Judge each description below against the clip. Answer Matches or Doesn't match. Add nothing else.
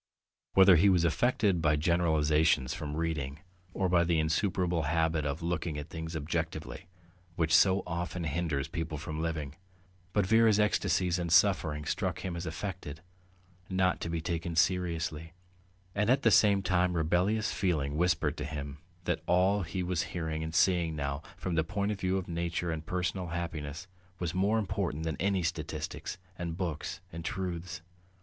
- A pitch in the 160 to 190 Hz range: Doesn't match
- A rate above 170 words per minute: Doesn't match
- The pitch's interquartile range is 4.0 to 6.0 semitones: Doesn't match